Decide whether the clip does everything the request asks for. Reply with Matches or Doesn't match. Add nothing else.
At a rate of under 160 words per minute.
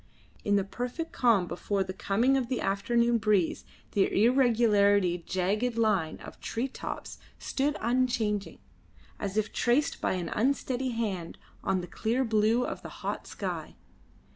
Matches